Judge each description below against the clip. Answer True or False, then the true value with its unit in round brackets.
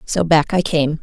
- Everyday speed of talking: False (235 wpm)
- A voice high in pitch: False (155 Hz)